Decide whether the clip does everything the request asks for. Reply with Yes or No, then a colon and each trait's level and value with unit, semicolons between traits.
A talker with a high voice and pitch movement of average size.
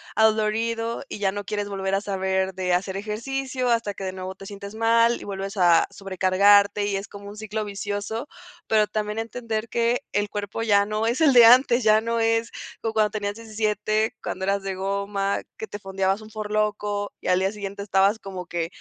No: high, 205 Hz; narrow, 2.1 semitones